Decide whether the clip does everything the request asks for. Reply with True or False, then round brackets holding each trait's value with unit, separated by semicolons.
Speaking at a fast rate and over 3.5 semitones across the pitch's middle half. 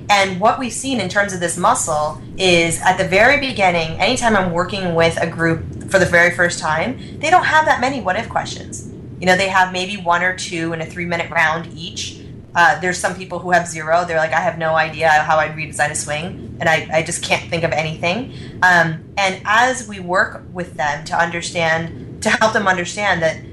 False (220 wpm; 2.9 semitones)